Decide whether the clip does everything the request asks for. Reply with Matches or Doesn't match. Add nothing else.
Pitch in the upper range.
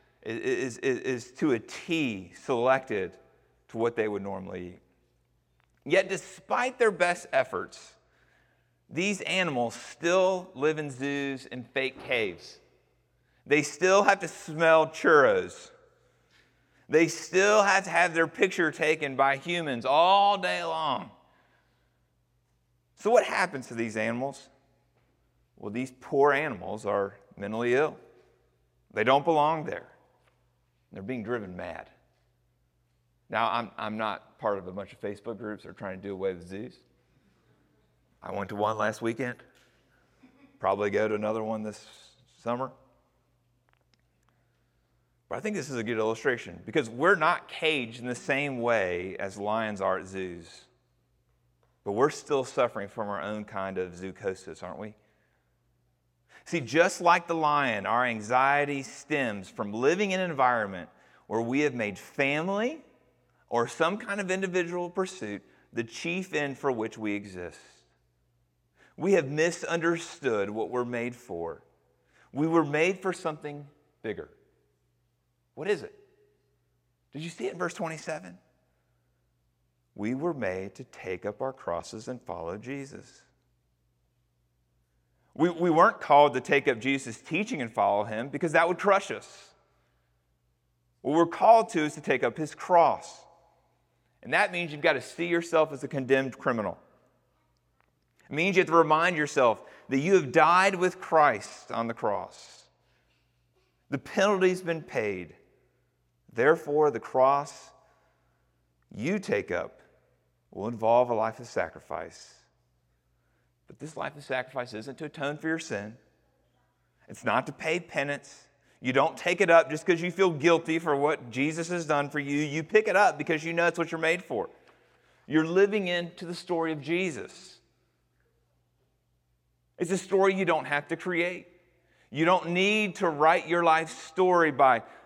Doesn't match